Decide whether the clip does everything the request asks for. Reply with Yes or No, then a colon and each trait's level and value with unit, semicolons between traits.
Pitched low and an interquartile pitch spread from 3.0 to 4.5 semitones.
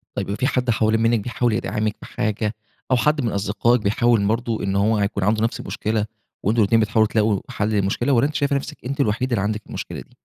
No: low, 110 Hz; narrow, 2.4 semitones